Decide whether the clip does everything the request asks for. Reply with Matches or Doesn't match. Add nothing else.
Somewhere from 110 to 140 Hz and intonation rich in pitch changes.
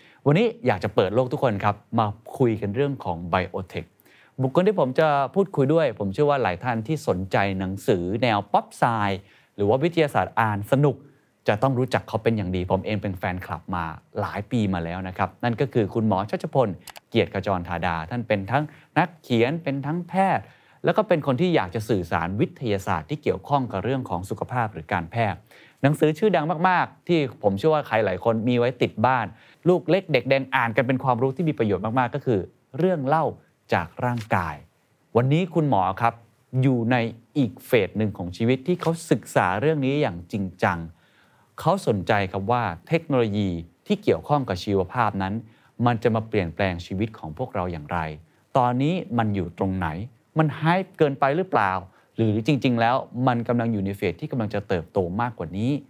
Matches